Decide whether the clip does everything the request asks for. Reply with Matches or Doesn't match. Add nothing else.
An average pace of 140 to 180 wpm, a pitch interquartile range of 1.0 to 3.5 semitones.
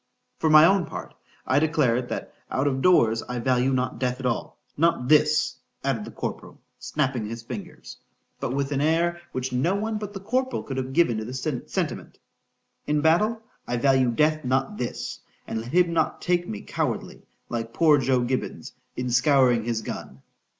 Doesn't match